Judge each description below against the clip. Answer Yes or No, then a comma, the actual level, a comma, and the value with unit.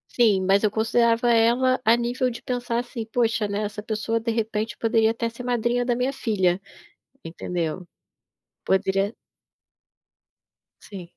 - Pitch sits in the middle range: No, high, 225 Hz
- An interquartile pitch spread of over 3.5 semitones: No, narrow, 2.5 semitones